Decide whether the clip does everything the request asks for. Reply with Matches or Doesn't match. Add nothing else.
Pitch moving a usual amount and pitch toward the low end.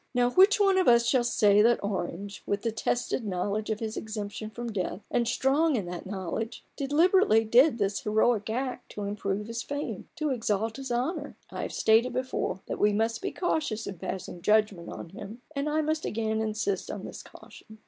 Doesn't match